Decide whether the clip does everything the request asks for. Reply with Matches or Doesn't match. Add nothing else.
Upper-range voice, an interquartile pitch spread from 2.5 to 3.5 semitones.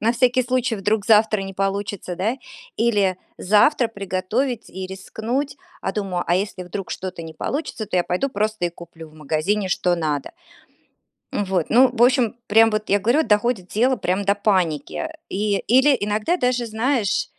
Doesn't match